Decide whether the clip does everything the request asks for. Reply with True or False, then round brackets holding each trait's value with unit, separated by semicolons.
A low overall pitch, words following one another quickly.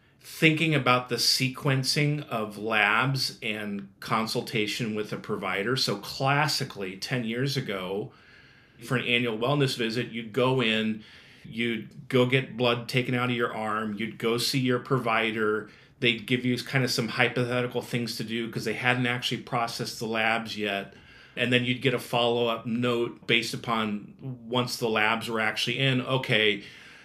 False (120 Hz; 160 wpm)